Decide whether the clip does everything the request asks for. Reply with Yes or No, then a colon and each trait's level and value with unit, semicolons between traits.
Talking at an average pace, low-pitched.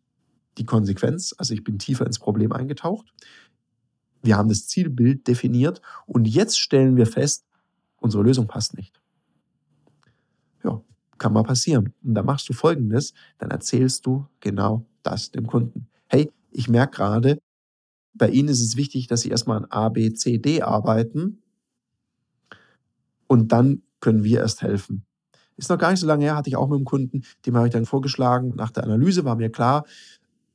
Yes: average, 170 wpm; low, 125 Hz